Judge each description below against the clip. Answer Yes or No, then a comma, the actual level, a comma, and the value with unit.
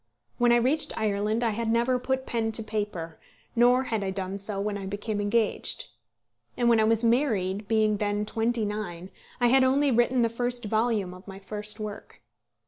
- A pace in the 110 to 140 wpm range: No, average, 190 wpm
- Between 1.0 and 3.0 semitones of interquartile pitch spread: Yes, average, 2.7 semitones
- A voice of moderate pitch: No, high, 220 Hz